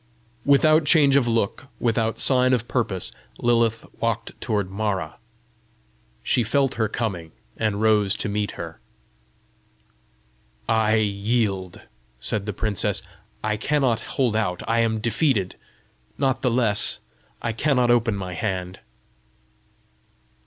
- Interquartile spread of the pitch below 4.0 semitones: Yes, average, 3.0 semitones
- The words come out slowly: Yes, slow, 120 wpm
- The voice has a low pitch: Yes, low, 110 Hz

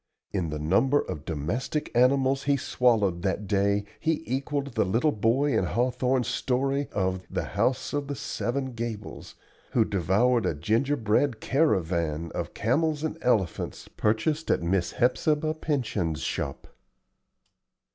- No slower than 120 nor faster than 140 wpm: Yes, slow, 135 wpm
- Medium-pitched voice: No, low, 120 Hz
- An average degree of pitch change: No, wide, 6.1 semitones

